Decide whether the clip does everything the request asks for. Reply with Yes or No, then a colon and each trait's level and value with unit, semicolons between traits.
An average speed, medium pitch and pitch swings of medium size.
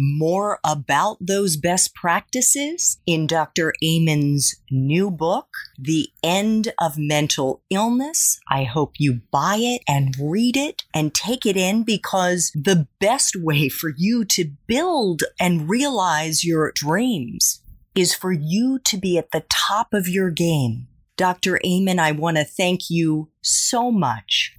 Yes: average, 145 wpm; medium, 175 Hz; average, 4.9 semitones